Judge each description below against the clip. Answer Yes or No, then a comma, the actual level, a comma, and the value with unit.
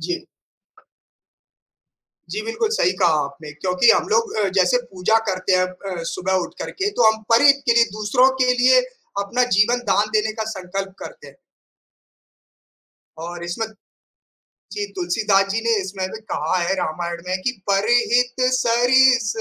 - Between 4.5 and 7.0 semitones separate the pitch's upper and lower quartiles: Yes, average, 5.0 semitones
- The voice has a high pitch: Yes, high, 215 Hz